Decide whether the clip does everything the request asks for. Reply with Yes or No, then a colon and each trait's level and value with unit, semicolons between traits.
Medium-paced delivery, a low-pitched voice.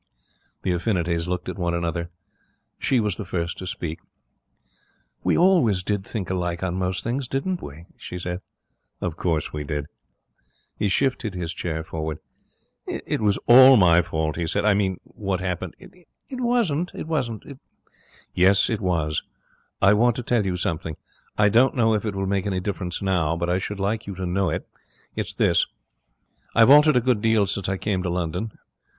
Yes: average, 180 wpm; very low, 95 Hz